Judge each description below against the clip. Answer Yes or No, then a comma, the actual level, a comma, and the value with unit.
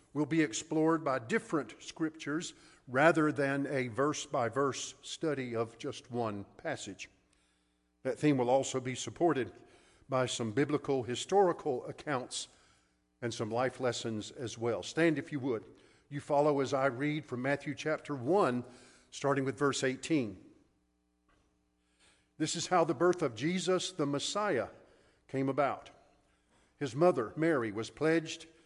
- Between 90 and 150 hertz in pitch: Yes, medium, 140 Hz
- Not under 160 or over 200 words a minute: No, average, 140 wpm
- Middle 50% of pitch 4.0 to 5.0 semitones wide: Yes, average, 4.5 semitones